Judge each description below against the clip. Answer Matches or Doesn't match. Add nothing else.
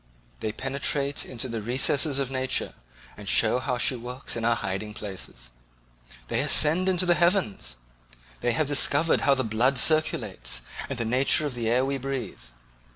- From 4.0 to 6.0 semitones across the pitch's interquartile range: Doesn't match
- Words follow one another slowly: Doesn't match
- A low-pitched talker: Matches